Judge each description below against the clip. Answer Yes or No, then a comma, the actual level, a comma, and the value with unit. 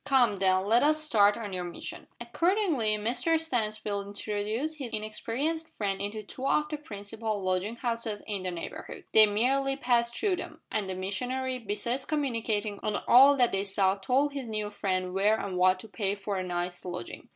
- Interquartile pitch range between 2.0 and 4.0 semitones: No, average, 4.4 semitones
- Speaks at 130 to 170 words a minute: No, average, 185 wpm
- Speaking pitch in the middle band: No, high, 215 Hz